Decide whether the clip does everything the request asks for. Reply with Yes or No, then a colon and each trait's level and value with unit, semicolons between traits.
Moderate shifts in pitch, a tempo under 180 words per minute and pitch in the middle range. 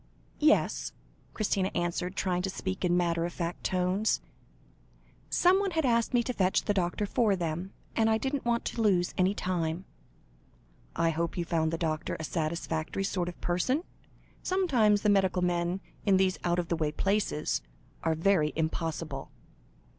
Yes: average, 3.6 semitones; average, 160 wpm; medium, 180 Hz